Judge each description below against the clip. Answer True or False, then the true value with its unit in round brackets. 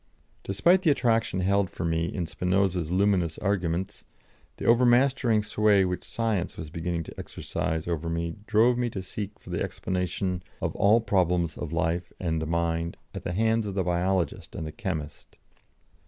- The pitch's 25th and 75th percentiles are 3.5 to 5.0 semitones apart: True (4.1 semitones)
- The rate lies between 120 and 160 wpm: False (170 wpm)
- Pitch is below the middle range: True (90 Hz)